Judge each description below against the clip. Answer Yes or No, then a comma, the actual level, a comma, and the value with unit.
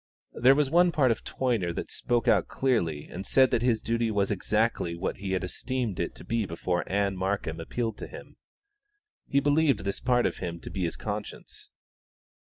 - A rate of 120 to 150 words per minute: No, average, 190 wpm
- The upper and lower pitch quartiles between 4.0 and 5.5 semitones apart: Yes, average, 5.1 semitones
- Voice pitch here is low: Yes, low, 110 Hz